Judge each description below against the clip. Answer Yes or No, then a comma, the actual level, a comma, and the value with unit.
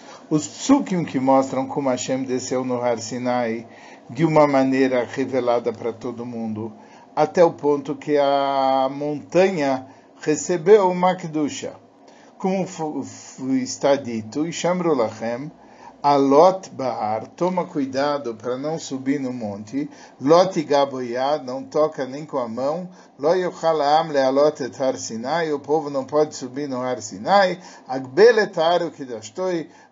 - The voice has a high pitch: No, medium, 140 Hz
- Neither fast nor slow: Yes, average, 135 wpm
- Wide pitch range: No, average, 4.0 semitones